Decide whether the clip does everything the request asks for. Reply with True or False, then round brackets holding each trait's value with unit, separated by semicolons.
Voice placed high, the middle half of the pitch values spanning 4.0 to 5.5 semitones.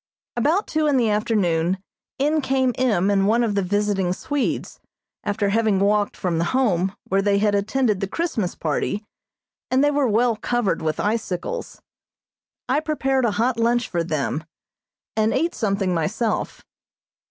True (215 Hz; 4.7 semitones)